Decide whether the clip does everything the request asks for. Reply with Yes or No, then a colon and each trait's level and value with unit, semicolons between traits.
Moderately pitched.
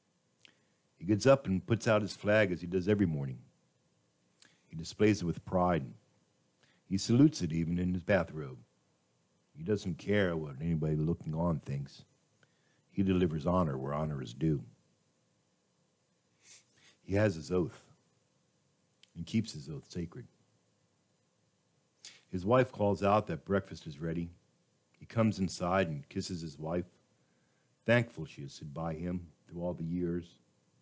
No: very low, 90 Hz